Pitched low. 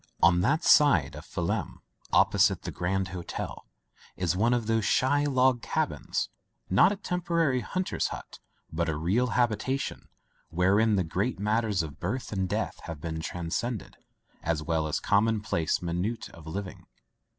Yes: low, 100 Hz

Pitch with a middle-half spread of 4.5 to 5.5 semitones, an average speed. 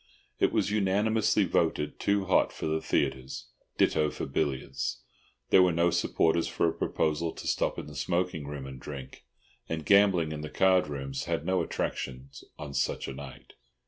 Yes: average, 4.9 semitones; average, 175 wpm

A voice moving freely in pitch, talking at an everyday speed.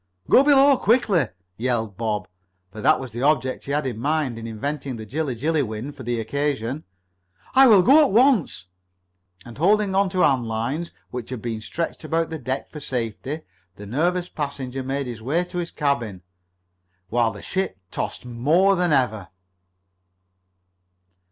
Yes: wide, 6.5 semitones; average, 170 wpm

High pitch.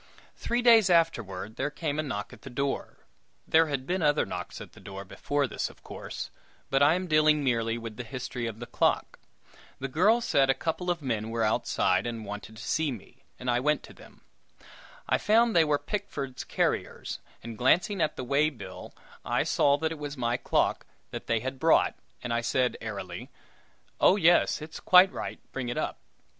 No: low, 135 Hz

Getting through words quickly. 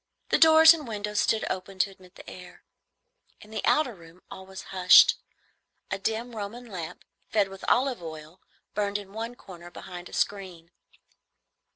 No: average, 165 wpm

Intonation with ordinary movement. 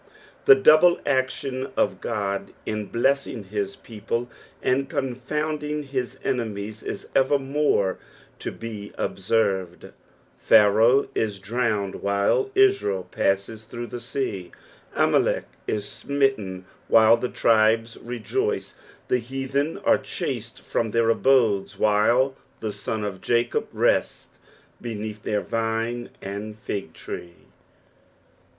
Yes: average, 4.3 semitones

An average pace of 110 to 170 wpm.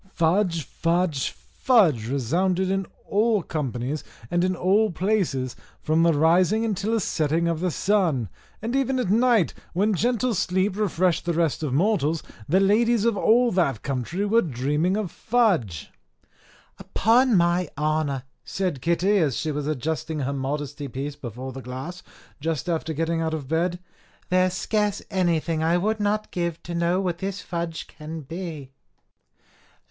Yes: average, 155 wpm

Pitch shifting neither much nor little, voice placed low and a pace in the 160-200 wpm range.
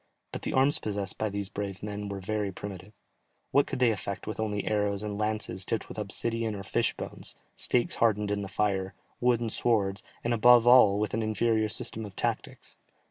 No: narrow, 2.1 semitones; low, 105 Hz; average, 190 wpm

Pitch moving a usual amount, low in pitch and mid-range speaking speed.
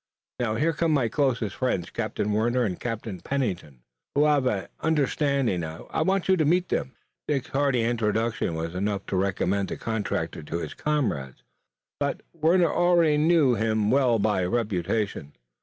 No: wide, 6.6 semitones; low, 120 Hz; average, 155 wpm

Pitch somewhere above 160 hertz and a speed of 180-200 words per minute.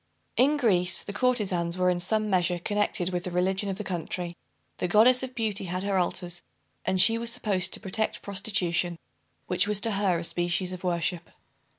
Yes: medium, 185 Hz; average, 190 wpm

